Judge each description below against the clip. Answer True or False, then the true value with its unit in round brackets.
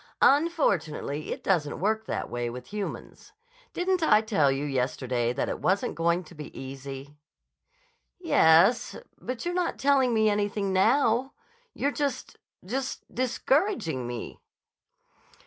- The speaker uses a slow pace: True (125 wpm)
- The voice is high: True (200 Hz)